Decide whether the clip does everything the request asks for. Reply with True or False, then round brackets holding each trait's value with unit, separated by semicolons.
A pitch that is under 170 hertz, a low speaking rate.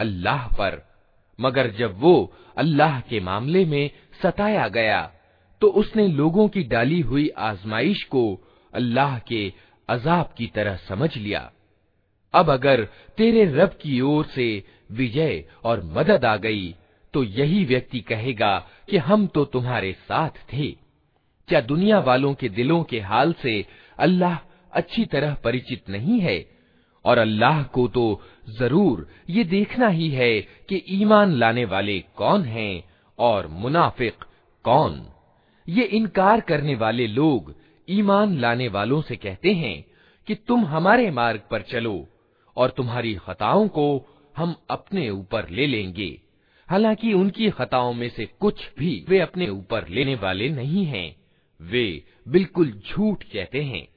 False (135 Hz; 140 wpm)